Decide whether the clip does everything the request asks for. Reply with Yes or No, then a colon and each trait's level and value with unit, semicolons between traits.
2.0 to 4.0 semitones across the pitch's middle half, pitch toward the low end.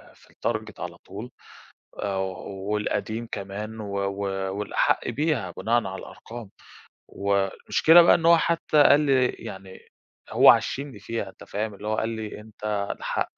Yes: average, 3.2 semitones; low, 105 Hz